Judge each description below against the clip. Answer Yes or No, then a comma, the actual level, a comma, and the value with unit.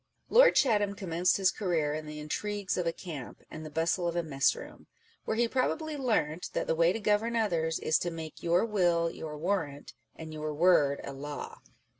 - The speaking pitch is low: No, medium, 170 Hz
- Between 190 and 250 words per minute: Yes, average, 200 wpm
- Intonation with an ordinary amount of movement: Yes, average, 4.9 semitones